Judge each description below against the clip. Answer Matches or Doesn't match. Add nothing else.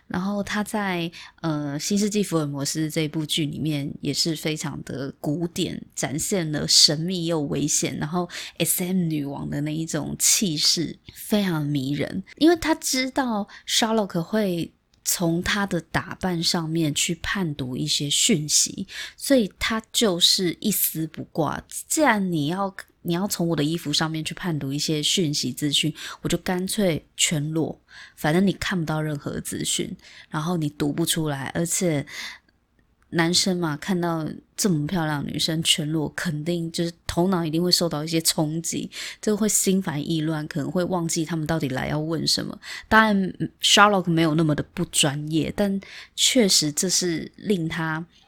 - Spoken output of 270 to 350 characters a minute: Doesn't match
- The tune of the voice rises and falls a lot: Doesn't match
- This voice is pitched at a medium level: Matches